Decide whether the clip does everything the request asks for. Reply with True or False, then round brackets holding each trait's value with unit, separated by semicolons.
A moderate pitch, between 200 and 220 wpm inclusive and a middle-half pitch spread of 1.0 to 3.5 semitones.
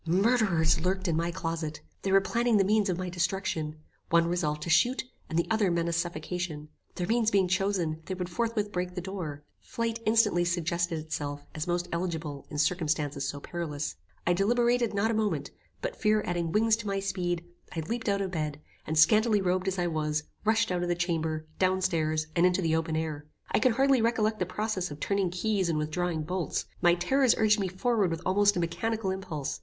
False (180 Hz; 205 wpm; 4.0 semitones)